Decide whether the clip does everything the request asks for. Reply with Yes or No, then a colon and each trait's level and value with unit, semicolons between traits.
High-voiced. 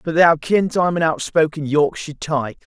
No: medium, 160 Hz